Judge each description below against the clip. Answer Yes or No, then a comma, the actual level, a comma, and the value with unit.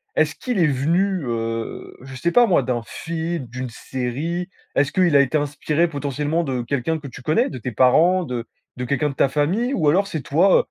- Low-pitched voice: No, medium, 145 Hz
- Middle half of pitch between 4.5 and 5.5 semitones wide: Yes, average, 4.9 semitones